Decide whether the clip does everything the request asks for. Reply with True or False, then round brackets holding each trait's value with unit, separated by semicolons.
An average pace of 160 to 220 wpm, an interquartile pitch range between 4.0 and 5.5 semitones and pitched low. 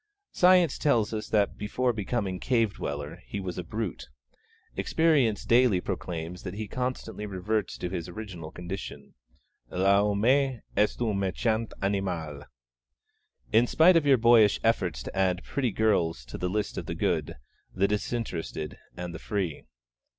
False (145 wpm; 4.3 semitones; 105 Hz)